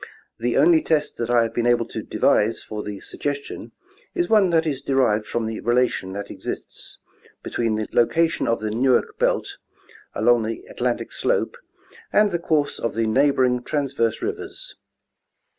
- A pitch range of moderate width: Yes, average, 4.4 semitones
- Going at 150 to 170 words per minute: Yes, average, 165 wpm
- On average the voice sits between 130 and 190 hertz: No, low, 120 Hz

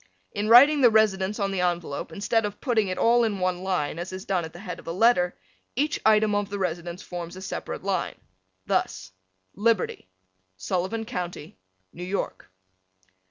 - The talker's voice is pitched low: No, high, 190 Hz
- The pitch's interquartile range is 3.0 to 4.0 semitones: Yes, average, 3.7 semitones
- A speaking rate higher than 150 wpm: Yes, average, 175 wpm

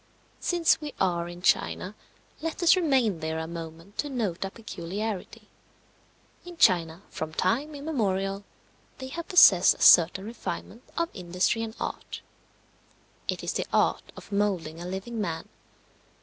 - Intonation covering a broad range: Yes, wide, 7.1 semitones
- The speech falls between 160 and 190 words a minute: No, average, 145 wpm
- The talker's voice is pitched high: Yes, high, 195 Hz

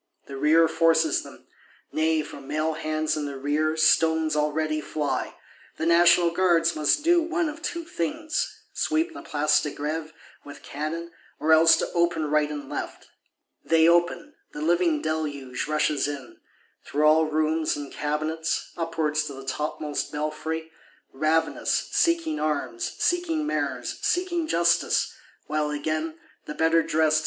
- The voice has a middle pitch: Yes, medium, 155 Hz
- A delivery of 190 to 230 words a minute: No, average, 145 wpm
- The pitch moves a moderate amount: No, narrow, 1.9 semitones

